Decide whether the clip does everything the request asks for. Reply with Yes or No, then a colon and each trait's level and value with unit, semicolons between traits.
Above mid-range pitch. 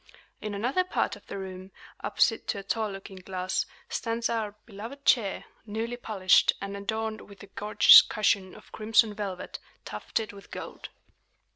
Yes: high, 205 Hz